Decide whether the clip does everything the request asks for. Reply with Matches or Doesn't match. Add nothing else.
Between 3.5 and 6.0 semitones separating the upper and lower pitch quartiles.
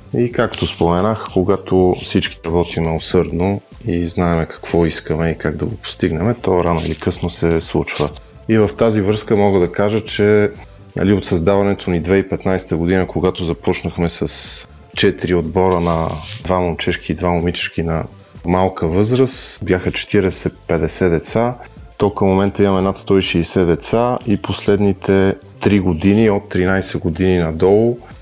Doesn't match